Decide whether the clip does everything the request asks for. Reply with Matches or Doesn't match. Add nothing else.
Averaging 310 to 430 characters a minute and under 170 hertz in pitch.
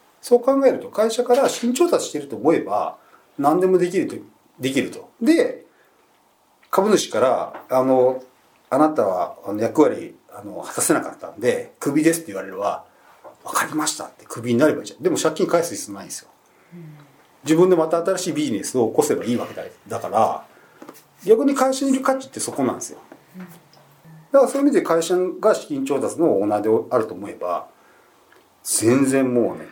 Doesn't match